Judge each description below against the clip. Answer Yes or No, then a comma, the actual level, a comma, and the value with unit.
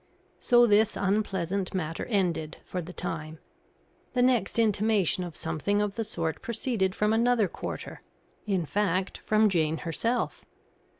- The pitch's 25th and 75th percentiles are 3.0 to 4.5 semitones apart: Yes, average, 4.2 semitones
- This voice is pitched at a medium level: No, high, 195 Hz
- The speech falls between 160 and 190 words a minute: No, slow, 135 wpm